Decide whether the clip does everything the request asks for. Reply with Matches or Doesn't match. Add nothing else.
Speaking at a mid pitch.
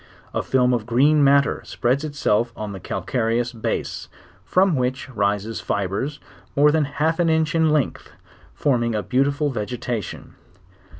Doesn't match